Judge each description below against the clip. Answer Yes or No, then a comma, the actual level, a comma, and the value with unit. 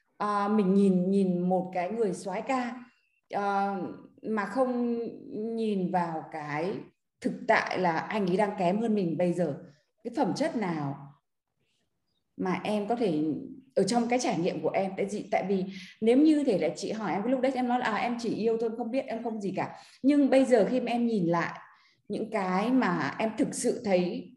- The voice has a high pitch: Yes, high, 215 Hz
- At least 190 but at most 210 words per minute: Yes, average, 205 wpm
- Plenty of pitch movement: No, average, 4.7 semitones